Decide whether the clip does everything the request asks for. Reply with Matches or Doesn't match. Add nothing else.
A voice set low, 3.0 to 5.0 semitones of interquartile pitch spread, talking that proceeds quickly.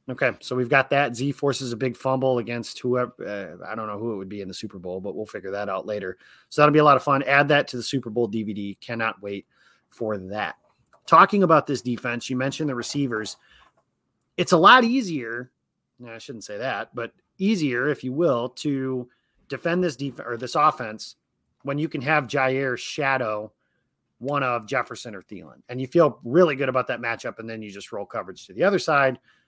Matches